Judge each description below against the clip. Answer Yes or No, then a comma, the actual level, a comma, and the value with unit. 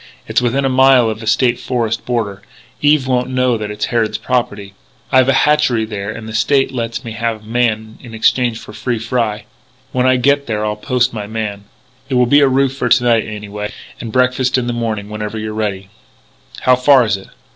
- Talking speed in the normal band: No, fast, 210 wpm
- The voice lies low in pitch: Yes, low, 115 Hz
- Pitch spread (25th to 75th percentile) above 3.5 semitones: No, average, 2.9 semitones